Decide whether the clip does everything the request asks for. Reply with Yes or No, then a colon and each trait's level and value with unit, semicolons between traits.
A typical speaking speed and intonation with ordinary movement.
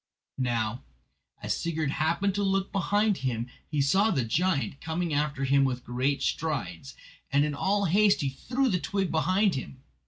No: average, 165 wpm; wide, 6.2 semitones